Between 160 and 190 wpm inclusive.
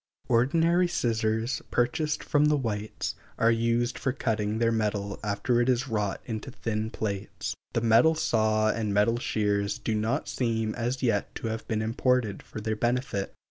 Yes: average, 165 wpm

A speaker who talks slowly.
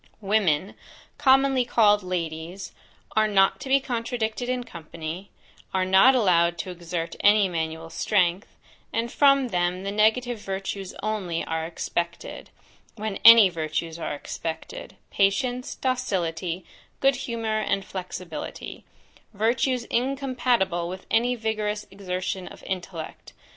Yes: slow, 120 wpm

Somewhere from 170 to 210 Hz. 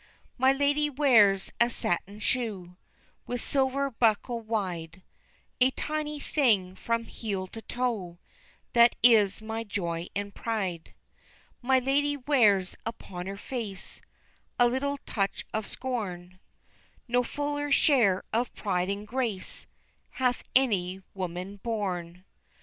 No: high, 225 Hz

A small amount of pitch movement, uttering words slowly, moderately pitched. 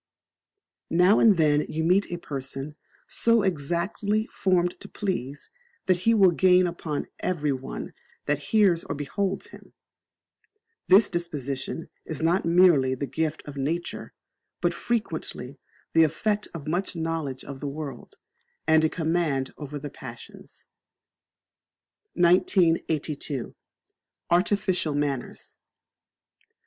No: average, 4.1 semitones; slow, 115 wpm; medium, 165 Hz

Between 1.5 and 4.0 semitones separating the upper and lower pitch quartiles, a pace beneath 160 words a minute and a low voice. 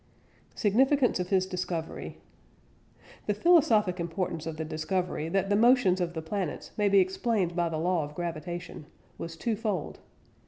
No: average, 3.7 semitones; average, 150 wpm; medium, 185 Hz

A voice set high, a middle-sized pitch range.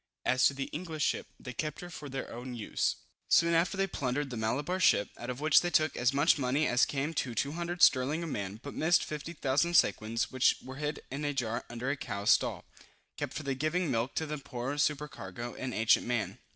No: medium, 140 Hz; average, 4.0 semitones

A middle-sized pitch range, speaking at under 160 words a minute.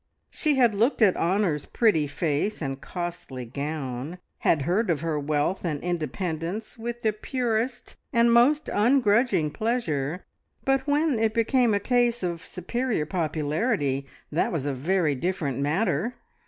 No: wide, 7.4 semitones; average, 140 wpm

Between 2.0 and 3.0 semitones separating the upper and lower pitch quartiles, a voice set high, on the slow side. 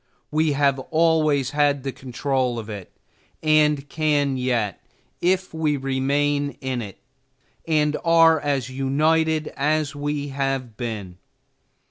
No: average, 2.7 semitones; medium, 145 Hz; slow, 120 wpm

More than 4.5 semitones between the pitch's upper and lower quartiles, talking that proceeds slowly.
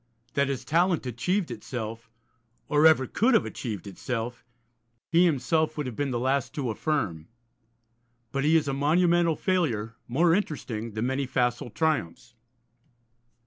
No: average, 5.1 semitones; average, 145 wpm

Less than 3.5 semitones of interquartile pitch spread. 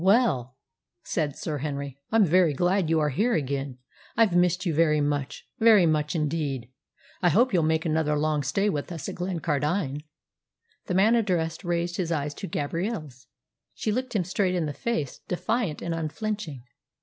No: average, 4.4 semitones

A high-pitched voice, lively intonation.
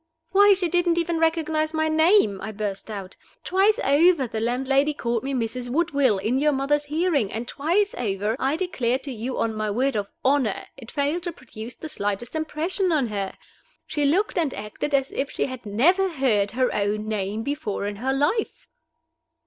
Yes: very high, 270 Hz; wide, 6.4 semitones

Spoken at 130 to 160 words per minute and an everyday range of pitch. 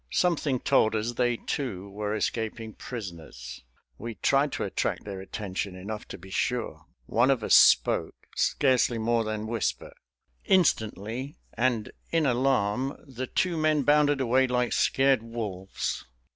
Yes: average, 140 wpm; average, 4.0 semitones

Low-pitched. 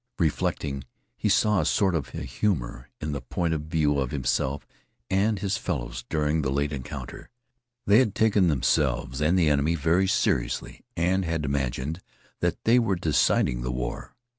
Yes: very low, 75 Hz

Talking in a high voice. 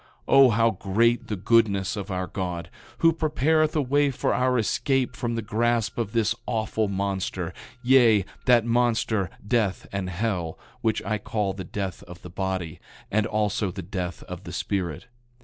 No: low, 105 Hz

